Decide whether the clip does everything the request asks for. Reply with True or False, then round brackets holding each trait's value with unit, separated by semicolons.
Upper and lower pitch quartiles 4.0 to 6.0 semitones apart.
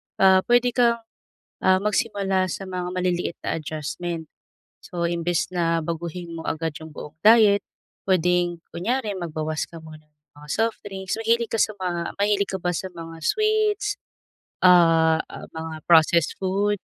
False (3.6 semitones)